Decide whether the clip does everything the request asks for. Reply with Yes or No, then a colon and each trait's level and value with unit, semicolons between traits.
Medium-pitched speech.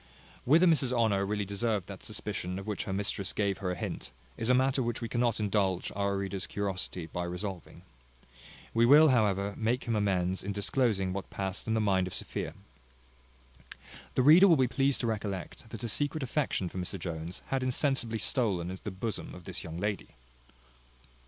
No: low, 105 Hz